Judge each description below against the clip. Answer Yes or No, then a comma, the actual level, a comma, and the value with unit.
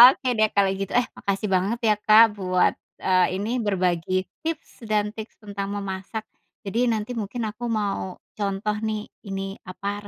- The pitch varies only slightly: Yes, narrow, 2.1 semitones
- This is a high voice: Yes, high, 205 Hz